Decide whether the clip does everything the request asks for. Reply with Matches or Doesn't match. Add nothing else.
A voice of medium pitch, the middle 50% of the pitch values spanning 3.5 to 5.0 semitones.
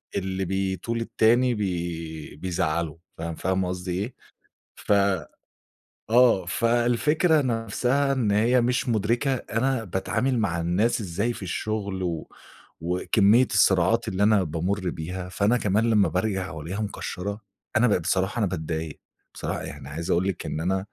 Doesn't match